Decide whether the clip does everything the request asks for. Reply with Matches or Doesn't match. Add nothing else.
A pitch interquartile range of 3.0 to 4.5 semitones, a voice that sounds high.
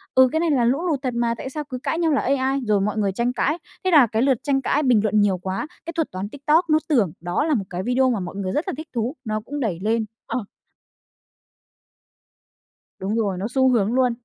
Doesn't match